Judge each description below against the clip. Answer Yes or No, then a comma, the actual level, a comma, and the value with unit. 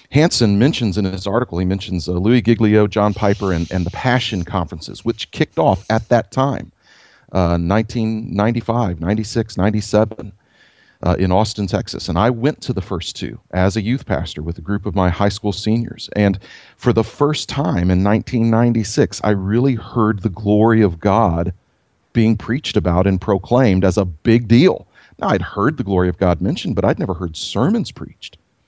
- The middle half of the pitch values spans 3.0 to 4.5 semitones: Yes, average, 3.6 semitones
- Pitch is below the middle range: Yes, low, 105 Hz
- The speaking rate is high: No, average, 180 wpm